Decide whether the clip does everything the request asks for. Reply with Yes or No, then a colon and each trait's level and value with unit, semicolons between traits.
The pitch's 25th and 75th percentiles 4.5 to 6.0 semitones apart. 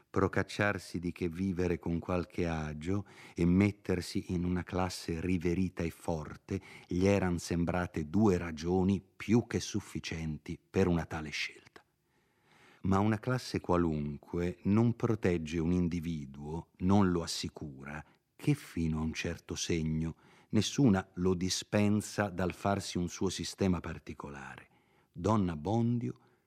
No: average, 3.1 semitones